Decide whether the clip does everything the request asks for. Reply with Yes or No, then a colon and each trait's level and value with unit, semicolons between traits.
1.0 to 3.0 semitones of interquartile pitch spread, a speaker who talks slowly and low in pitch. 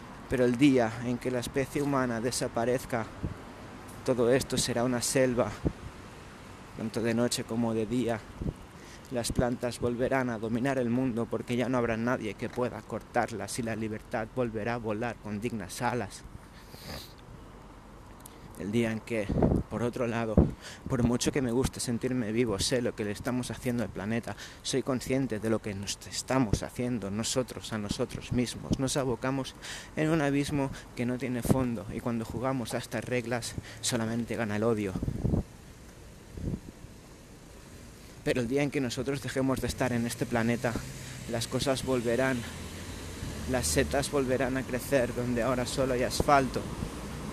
No: narrow, 2.4 semitones; average, 155 wpm; low, 120 Hz